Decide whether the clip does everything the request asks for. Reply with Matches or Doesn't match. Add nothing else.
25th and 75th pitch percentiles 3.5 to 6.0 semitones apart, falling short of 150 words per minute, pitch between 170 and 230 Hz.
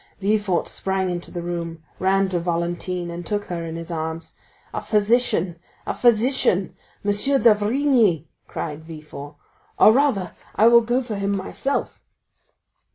Matches